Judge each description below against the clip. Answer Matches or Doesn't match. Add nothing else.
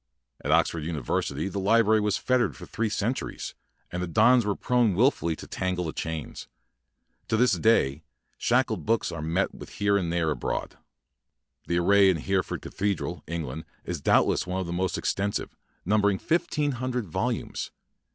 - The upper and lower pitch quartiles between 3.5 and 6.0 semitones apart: Matches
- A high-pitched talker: Doesn't match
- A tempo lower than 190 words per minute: Matches